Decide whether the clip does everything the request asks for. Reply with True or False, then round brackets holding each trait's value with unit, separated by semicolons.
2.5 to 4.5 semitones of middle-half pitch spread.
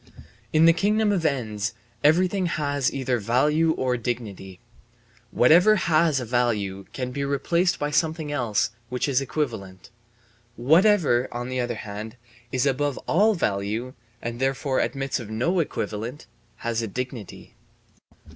False (4.9 semitones)